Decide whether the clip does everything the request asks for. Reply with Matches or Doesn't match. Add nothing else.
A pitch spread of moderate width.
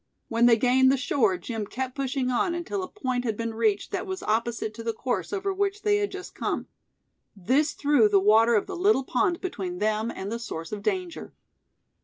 Doesn't match